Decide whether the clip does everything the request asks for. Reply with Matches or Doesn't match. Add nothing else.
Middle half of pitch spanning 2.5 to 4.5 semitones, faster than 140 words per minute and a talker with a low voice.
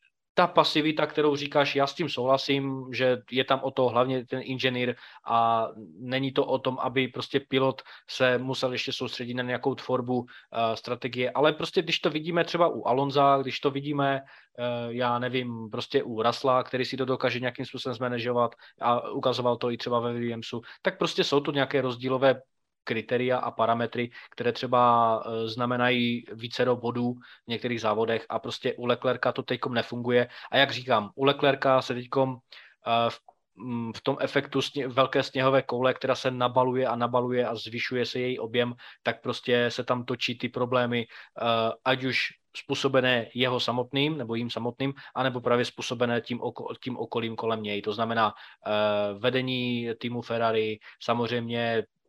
Doesn't match